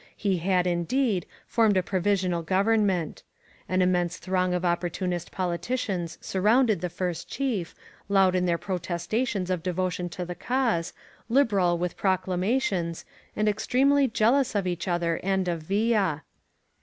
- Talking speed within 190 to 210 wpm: No, average, 150 wpm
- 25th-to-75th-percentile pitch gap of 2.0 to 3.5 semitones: Yes, average, 3.2 semitones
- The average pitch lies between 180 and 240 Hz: Yes, medium, 185 Hz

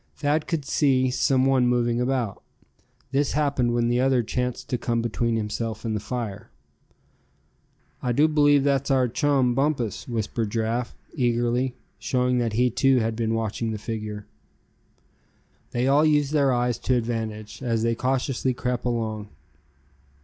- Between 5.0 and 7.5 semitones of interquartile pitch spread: No, average, 2.7 semitones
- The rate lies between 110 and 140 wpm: No, average, 150 wpm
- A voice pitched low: Yes, low, 125 Hz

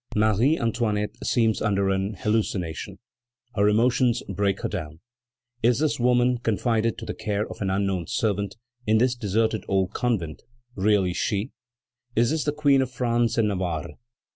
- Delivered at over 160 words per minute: No, average, 155 wpm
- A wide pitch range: No, average, 3.5 semitones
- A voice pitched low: Yes, low, 110 Hz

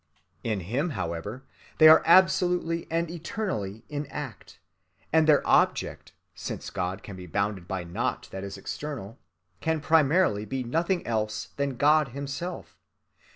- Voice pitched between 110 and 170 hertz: Yes, medium, 140 Hz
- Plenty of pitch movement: Yes, wide, 8.1 semitones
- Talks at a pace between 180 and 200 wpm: No, average, 140 wpm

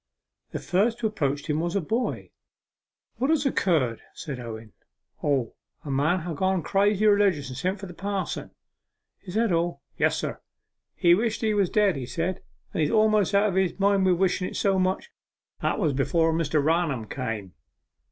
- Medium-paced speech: Yes, average, 180 wpm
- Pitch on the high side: No, medium, 180 Hz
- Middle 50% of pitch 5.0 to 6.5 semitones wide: Yes, wide, 5.5 semitones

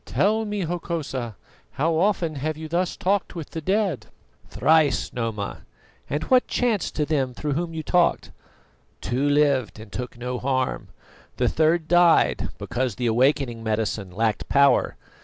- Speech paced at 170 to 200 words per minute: No, average, 150 wpm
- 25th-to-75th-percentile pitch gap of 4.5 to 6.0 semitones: Yes, wide, 5.5 semitones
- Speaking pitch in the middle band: Yes, medium, 150 Hz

